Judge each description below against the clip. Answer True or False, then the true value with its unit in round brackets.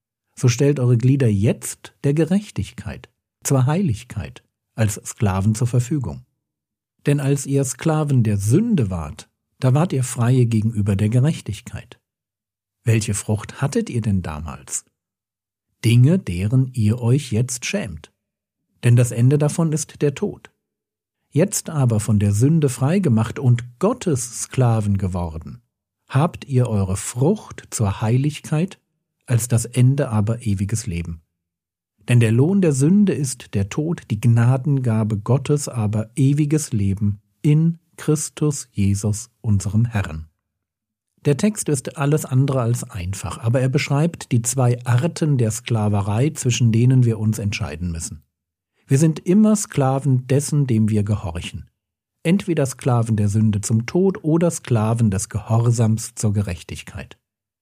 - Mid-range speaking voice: False (120 Hz)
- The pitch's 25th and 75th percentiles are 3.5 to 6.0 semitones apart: True (5.2 semitones)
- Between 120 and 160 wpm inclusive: True (135 wpm)